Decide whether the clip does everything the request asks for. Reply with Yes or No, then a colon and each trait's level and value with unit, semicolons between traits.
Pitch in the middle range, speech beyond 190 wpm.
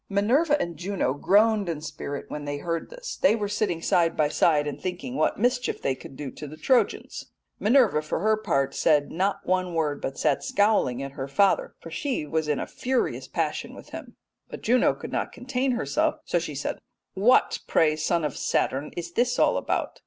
Yes: medium, 180 Hz; average, 200 wpm